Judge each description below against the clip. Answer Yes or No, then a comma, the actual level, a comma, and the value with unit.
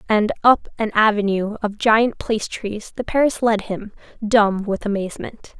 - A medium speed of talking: Yes, average, 160 wpm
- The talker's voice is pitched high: Yes, high, 215 Hz